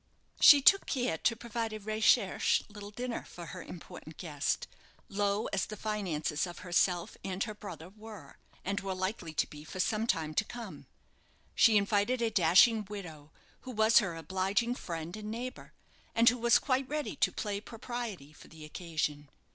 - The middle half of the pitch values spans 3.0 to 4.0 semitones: No, average, 4.6 semitones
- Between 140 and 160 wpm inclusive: No, average, 170 wpm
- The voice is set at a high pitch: Yes, high, 205 Hz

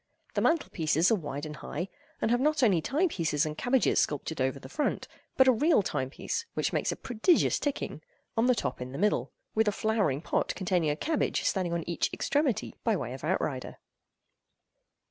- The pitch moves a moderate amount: No, wide, 8.8 semitones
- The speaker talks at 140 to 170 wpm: No, average, 195 wpm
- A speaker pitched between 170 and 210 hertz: Yes, high, 190 Hz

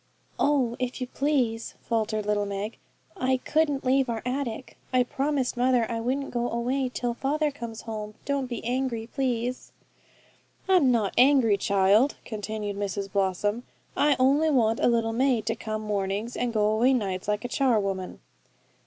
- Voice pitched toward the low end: No, high, 235 Hz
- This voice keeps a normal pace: Yes, average, 160 wpm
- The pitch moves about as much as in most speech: Yes, average, 3.6 semitones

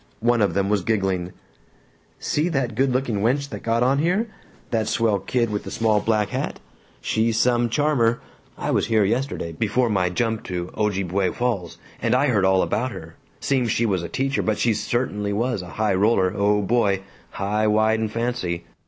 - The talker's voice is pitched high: No, low, 110 Hz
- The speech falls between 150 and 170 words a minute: No, average, 190 wpm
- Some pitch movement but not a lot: Yes, average, 3.5 semitones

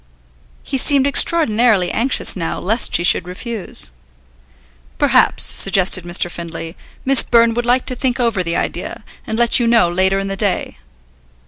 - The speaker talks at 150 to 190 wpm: Yes, average, 155 wpm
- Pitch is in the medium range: No, high, 220 Hz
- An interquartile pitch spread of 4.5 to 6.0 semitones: Yes, average, 5.0 semitones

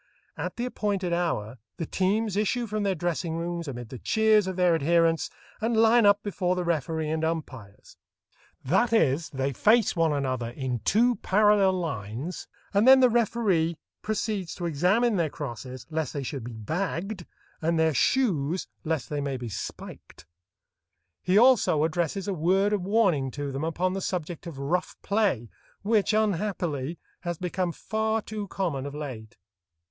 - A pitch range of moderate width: No, wide, 5.9 semitones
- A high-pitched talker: No, medium, 175 Hz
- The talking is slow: No, average, 165 wpm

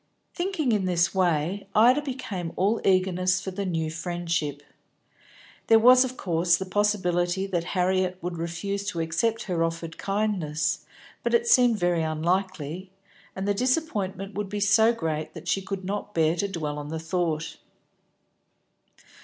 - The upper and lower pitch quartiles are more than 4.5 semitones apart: No, average, 3.6 semitones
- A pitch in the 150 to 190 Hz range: Yes, medium, 185 Hz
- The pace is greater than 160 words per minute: No, average, 155 wpm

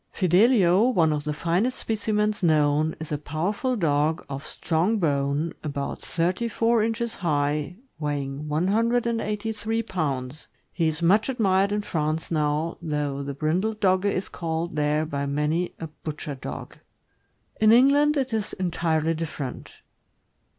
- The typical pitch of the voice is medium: Yes, medium, 165 Hz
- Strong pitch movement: Yes, wide, 5.9 semitones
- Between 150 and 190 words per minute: No, slow, 135 wpm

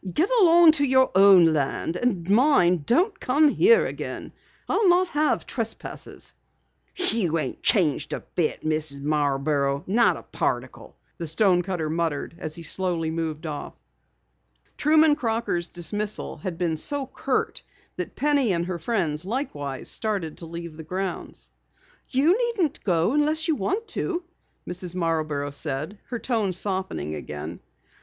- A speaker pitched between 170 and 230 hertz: Yes, medium, 185 Hz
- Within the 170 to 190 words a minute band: No, average, 140 wpm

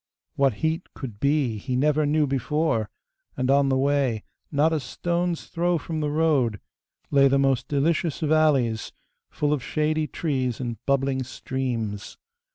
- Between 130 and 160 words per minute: Yes, average, 150 wpm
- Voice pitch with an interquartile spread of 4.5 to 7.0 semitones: No, average, 3.2 semitones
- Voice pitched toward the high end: No, medium, 140 Hz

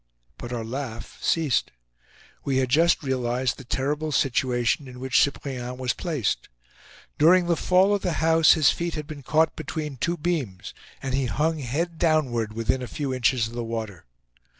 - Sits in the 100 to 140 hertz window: Yes, low, 135 Hz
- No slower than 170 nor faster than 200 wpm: Yes, average, 175 wpm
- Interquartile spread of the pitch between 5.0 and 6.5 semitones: No, average, 4.4 semitones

